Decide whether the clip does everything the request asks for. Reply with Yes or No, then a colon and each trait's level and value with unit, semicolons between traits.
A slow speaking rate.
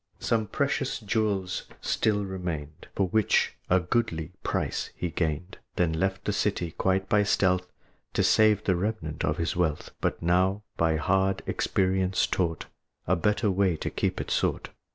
No: average, 155 wpm